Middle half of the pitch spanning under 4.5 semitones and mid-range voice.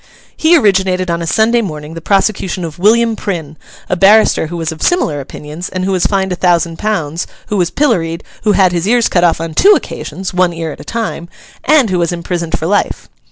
Yes: average, 3.9 semitones; medium, 180 Hz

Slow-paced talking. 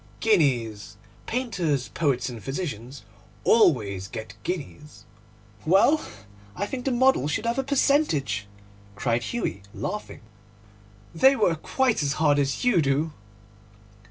Yes: slow, 120 wpm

